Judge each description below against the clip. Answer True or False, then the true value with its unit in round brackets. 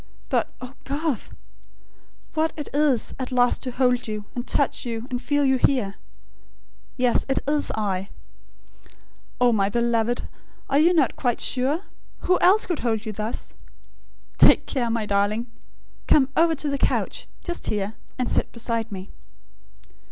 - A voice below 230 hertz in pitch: False (250 Hz)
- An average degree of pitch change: True (4.1 semitones)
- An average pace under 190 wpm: True (150 wpm)